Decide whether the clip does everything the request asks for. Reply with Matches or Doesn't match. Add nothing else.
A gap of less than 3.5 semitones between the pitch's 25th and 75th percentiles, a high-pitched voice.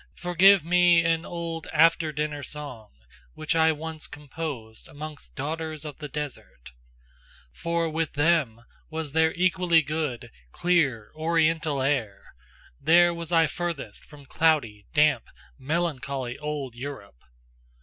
Doesn't match